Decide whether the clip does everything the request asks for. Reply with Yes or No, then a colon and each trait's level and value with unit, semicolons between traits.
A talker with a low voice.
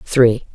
Yes: low, 120 Hz